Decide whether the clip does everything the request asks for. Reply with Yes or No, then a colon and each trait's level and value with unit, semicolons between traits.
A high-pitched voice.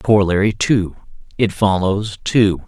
No: low, 100 Hz